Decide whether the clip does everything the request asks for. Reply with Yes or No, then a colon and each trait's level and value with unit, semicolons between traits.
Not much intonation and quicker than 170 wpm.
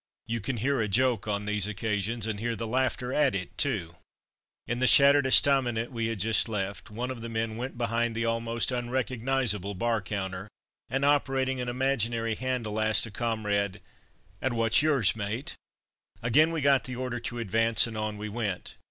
No: average, 3.2 semitones; average, 180 wpm